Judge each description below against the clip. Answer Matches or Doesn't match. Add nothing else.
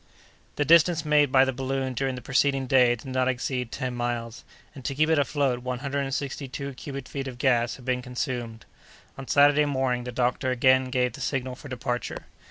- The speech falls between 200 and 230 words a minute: Matches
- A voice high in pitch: Doesn't match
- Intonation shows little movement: Matches